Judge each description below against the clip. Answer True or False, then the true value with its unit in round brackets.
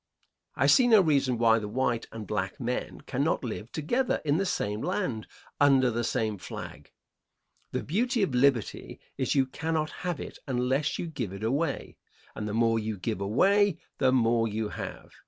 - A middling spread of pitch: False (5.9 semitones)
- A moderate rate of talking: True (175 wpm)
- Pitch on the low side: True (125 Hz)